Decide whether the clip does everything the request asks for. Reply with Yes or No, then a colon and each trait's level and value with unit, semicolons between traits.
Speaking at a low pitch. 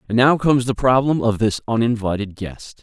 Yes: low, 120 Hz